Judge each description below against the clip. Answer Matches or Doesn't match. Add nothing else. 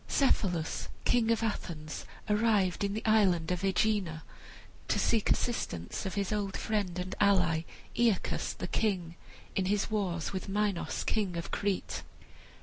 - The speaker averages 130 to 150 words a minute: Matches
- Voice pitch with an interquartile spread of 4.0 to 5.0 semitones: Doesn't match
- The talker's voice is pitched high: Matches